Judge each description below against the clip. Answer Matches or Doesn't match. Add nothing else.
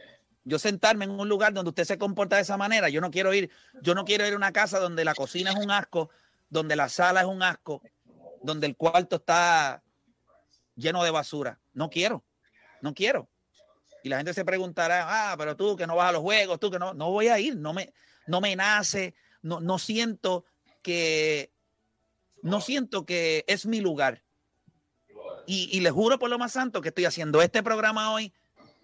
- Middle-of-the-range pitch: Matches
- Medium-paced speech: Doesn't match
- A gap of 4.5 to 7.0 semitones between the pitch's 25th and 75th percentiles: Doesn't match